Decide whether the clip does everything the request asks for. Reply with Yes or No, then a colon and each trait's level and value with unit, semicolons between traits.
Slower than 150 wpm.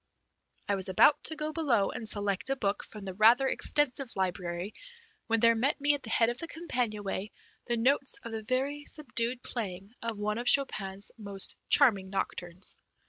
No: average, 185 wpm